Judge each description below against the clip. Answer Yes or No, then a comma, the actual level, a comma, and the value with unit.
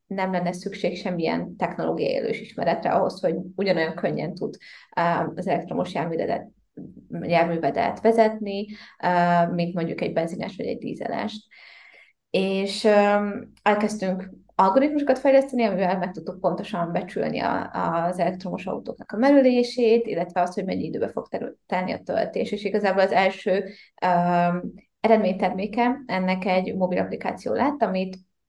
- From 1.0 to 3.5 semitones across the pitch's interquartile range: No, average, 3.9 semitones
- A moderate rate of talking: Yes, average, 120 wpm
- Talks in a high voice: Yes, high, 195 Hz